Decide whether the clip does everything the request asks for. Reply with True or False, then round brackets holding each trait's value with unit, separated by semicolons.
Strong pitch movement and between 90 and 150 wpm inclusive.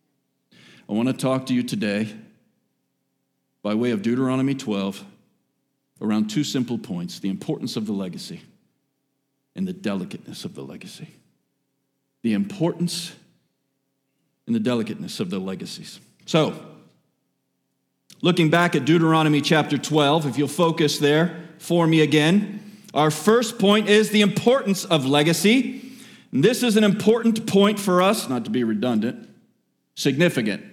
True (6.8 semitones; 135 wpm)